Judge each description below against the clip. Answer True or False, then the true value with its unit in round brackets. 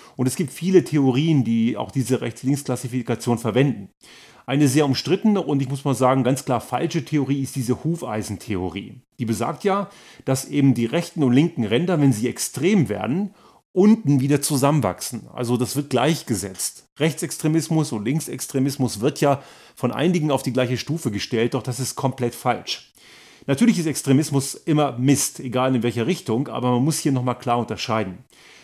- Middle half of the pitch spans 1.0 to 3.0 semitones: False (3.7 semitones)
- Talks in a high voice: False (135 Hz)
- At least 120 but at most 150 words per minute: False (165 wpm)